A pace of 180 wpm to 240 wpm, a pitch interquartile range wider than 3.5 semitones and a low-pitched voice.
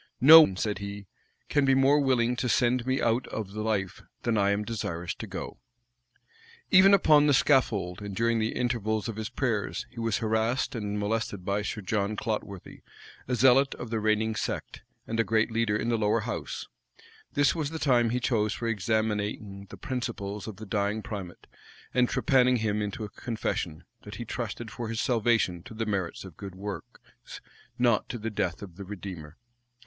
No: average, 185 wpm; average, 3.0 semitones; low, 110 Hz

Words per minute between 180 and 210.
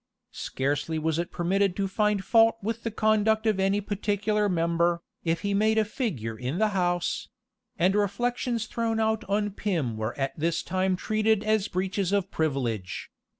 No: average, 165 wpm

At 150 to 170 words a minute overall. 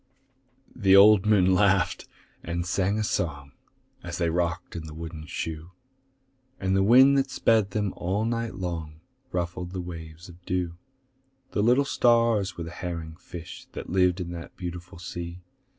Yes: average, 160 wpm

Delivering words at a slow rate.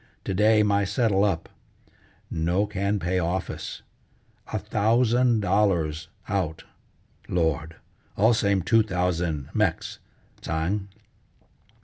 Yes: slow, 100 wpm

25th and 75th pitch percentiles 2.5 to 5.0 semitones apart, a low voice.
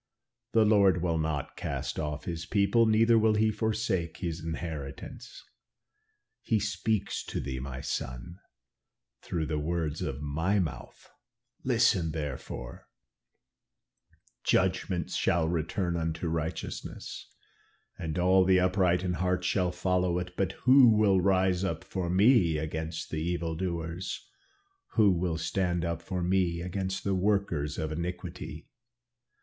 Yes: average, 2.9 semitones; very low, 90 Hz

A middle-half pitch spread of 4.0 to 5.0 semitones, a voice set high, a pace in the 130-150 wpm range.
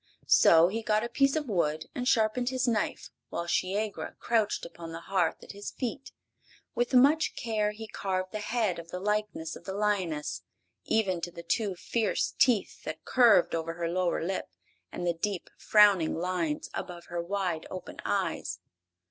No: average, 4.4 semitones; high, 195 Hz; average, 175 wpm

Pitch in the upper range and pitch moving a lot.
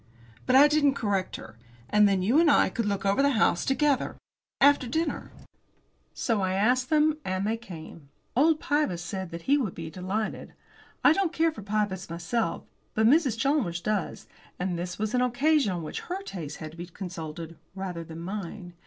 Yes: high, 210 Hz; wide, 7.7 semitones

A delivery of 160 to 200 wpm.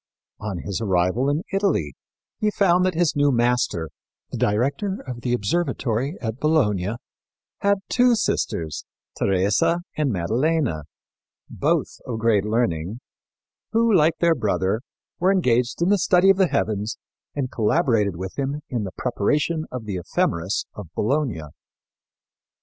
No: average, 140 wpm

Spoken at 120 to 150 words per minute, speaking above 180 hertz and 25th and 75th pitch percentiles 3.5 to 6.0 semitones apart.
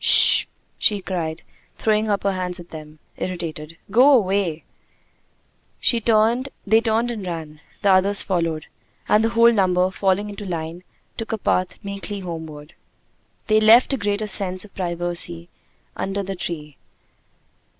Yes: average, 145 wpm; high, 190 Hz; average, 3.9 semitones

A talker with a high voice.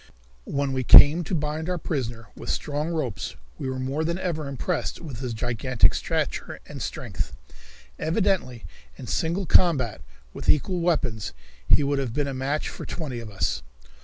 No: medium, 140 Hz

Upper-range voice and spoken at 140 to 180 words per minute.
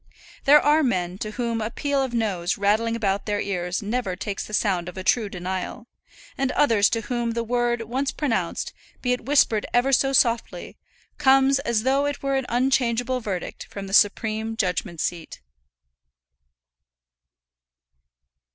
Yes: high, 230 Hz; average, 155 wpm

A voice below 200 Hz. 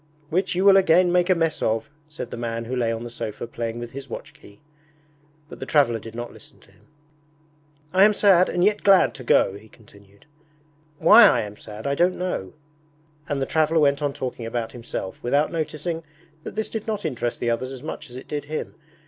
Yes: medium, 140 Hz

